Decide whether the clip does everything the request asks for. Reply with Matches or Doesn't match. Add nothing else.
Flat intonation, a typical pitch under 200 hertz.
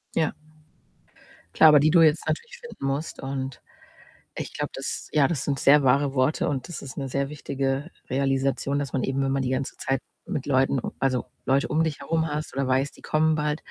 Matches